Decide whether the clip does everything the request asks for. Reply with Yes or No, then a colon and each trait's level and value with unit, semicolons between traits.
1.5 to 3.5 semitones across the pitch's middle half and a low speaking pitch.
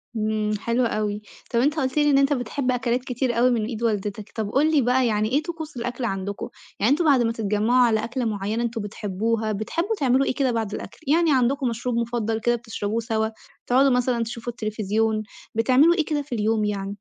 No: average, 3.1 semitones; high, 235 Hz